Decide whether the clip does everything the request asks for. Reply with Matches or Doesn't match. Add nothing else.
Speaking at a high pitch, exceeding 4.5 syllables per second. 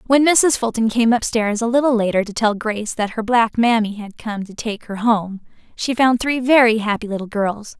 Matches